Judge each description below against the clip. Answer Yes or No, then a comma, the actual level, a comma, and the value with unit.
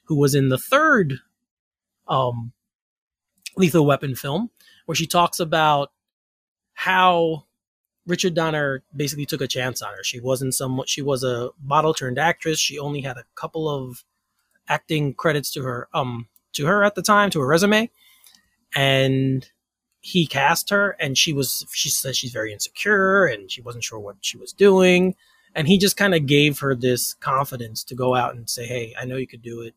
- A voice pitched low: No, medium, 145 Hz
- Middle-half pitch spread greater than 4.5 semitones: Yes, average, 4.9 semitones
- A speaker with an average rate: Yes, average, 185 wpm